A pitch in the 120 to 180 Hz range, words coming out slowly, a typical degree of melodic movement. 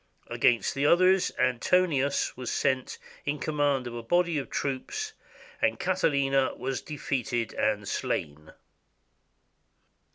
Yes: low, 135 Hz; slow, 110 wpm; average, 4.1 semitones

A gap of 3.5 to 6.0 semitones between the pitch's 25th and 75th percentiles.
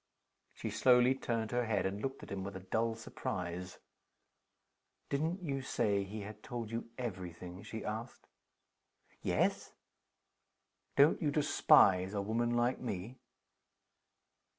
Yes: average, 3.9 semitones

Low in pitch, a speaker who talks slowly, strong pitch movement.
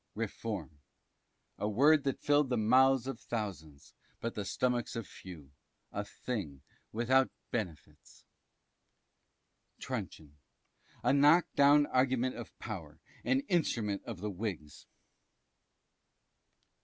Yes: low, 115 Hz; slow, 105 wpm; wide, 5.8 semitones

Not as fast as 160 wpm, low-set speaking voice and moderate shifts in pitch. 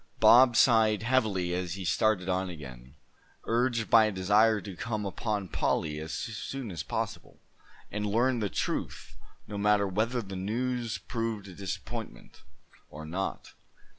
Yes: average, 145 wpm; low, 105 Hz; average, 3.7 semitones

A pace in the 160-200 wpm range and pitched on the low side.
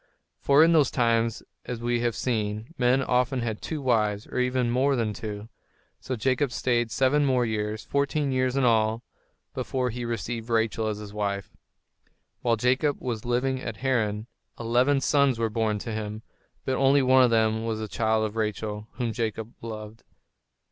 Yes: average, 175 wpm; low, 115 Hz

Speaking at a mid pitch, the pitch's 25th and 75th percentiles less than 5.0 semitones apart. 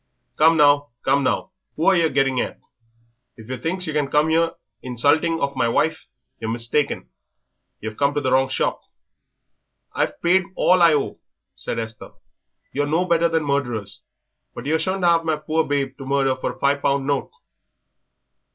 Yes: medium, 145 Hz; average, 3.4 semitones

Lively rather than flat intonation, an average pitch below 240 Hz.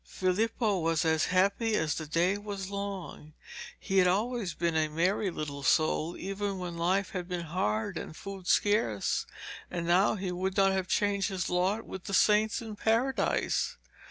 No: average, 3.1 semitones; medium, 185 Hz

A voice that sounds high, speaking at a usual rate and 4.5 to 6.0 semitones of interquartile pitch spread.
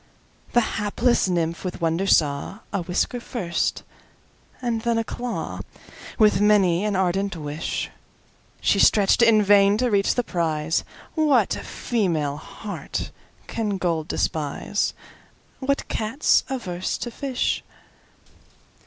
No: high, 200 Hz; slow, 100 wpm; average, 5.1 semitones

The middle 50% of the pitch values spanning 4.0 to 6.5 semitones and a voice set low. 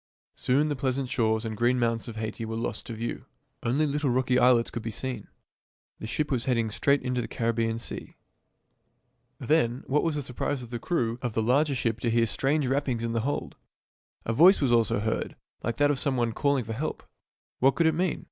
No: average, 3.4 semitones; low, 125 Hz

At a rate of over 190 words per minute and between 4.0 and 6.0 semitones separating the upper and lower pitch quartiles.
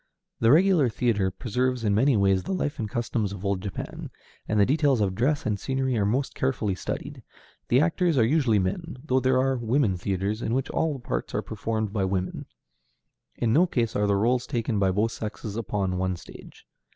Yes: average, 200 wpm; average, 4.7 semitones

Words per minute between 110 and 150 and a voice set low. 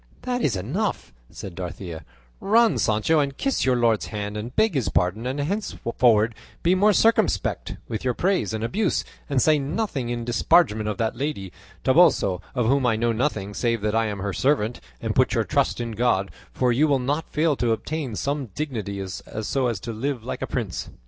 No: average, 195 wpm; low, 120 Hz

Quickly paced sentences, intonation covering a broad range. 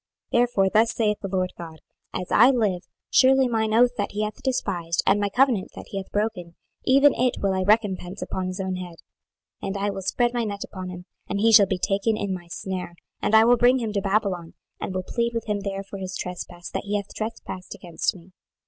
No: fast, 230 wpm; average, 3.4 semitones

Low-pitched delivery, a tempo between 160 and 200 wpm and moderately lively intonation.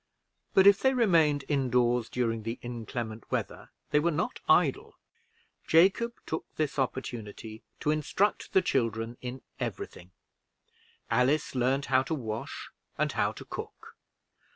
No: low, 130 Hz; average, 140 wpm; average, 4.9 semitones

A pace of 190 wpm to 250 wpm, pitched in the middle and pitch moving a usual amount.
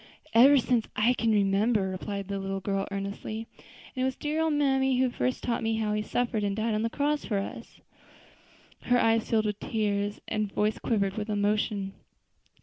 No: average, 195 wpm; high, 215 Hz; average, 3.3 semitones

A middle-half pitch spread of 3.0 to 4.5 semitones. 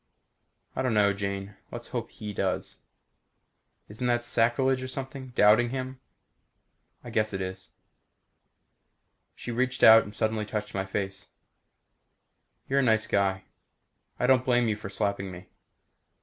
Yes: average, 3.9 semitones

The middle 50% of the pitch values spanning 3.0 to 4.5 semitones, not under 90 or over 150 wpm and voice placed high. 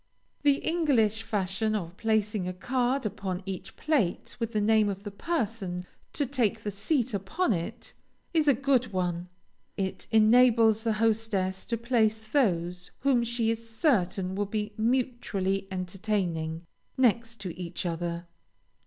Yes: average, 4.0 semitones; average, 140 wpm; high, 215 Hz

